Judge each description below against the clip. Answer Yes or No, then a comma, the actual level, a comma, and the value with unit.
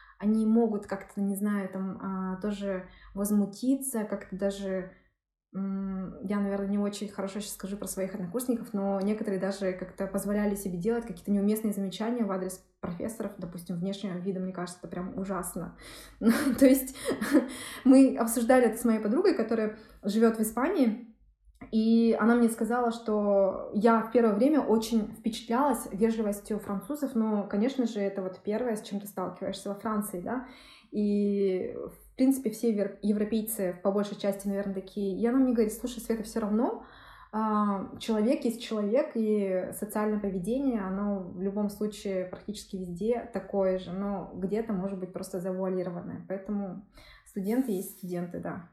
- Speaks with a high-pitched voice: Yes, high, 205 Hz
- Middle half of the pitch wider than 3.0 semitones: No, average, 2.7 semitones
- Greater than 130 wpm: Yes, average, 155 wpm